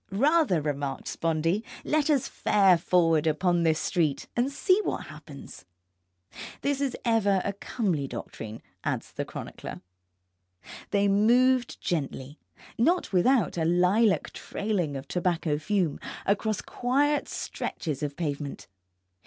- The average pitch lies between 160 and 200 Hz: Yes, medium, 185 Hz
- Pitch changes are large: Yes, wide, 6.9 semitones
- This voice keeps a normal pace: No, slow, 120 wpm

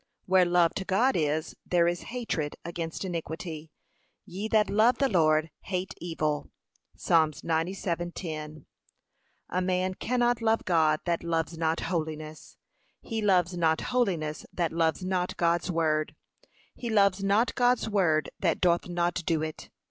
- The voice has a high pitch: No, medium, 175 Hz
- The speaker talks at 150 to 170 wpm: No, average, 140 wpm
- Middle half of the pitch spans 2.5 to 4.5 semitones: Yes, average, 3.1 semitones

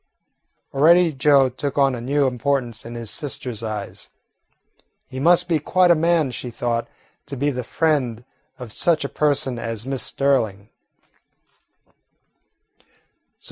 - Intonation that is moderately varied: Yes, average, 4.0 semitones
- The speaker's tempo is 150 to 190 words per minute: No, slow, 135 wpm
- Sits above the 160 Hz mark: No, low, 135 Hz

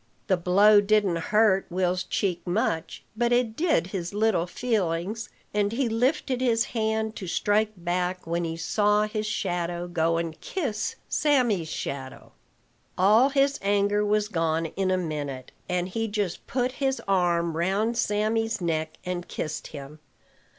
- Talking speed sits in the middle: Yes, average, 150 wpm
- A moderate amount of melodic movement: Yes, average, 4.2 semitones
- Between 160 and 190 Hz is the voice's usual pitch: No, high, 200 Hz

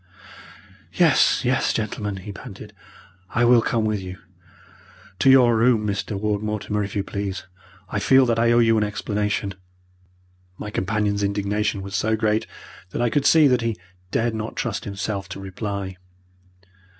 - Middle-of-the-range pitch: No, low, 105 Hz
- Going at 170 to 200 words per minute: No, average, 160 wpm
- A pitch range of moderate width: No, narrow, 2.2 semitones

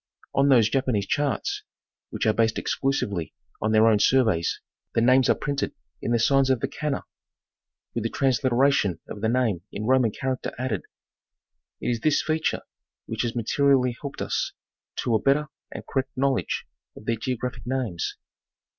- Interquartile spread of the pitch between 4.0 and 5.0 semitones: No, average, 3.4 semitones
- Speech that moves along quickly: No, average, 165 wpm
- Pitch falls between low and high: No, low, 125 Hz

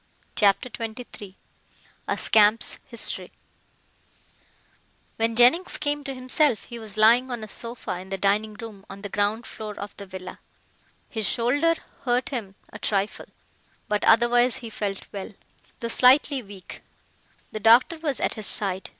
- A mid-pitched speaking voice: No, high, 225 Hz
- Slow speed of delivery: No, average, 150 wpm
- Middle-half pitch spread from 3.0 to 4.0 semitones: Yes, average, 3.4 semitones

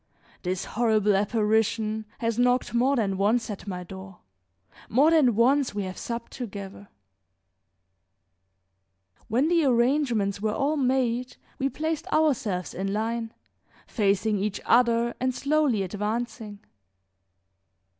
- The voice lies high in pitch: Yes, high, 230 Hz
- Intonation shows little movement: No, average, 3.7 semitones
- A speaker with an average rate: No, slow, 115 wpm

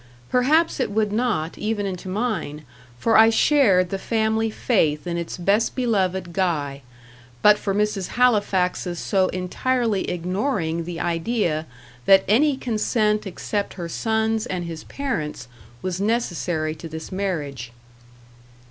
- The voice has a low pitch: No, high, 195 Hz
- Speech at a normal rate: No, slow, 130 wpm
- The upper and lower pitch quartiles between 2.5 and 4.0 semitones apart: No, average, 4.4 semitones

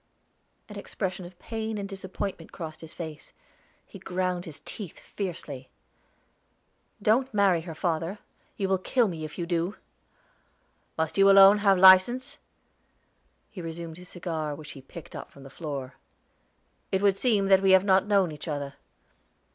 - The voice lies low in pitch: No, medium, 185 Hz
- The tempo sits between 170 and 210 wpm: No, average, 155 wpm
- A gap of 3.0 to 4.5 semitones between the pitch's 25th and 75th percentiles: Yes, average, 3.5 semitones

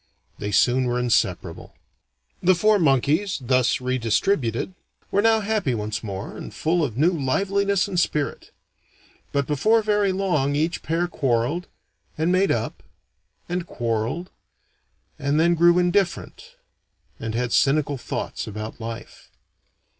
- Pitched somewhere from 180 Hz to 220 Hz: No, medium, 155 Hz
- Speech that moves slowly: Yes, slow, 130 wpm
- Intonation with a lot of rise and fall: Yes, wide, 7.0 semitones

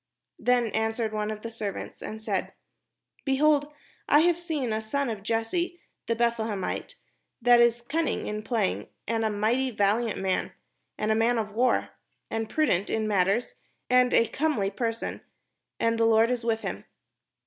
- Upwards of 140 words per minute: Yes, average, 165 wpm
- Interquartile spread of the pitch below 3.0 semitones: Yes, narrow, 2.5 semitones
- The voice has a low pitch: No, high, 230 Hz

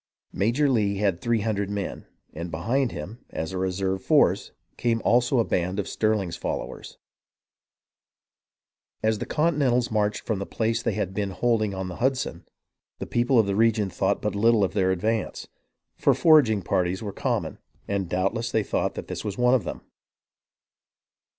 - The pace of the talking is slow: No, average, 170 wpm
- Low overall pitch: Yes, low, 105 Hz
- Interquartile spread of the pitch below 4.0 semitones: Yes, average, 3.5 semitones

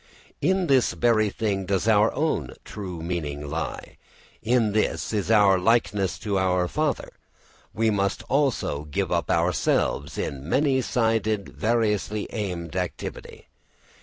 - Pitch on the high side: No, low, 105 Hz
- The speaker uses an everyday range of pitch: Yes, average, 3.9 semitones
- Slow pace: Yes, slow, 130 wpm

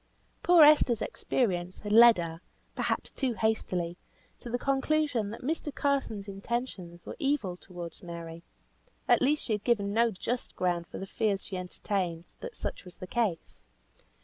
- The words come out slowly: No, average, 160 wpm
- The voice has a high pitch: Yes, high, 210 Hz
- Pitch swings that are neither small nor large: No, wide, 5.7 semitones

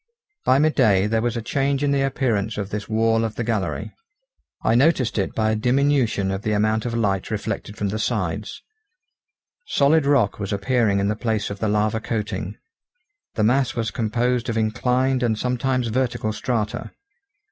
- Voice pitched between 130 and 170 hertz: No, low, 115 Hz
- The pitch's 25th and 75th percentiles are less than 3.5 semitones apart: Yes, average, 3.1 semitones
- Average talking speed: Yes, average, 180 wpm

